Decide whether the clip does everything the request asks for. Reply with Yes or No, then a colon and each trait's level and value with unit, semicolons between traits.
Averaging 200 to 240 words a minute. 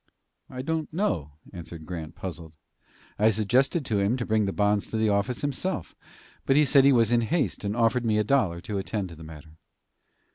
Yes: fast, 205 wpm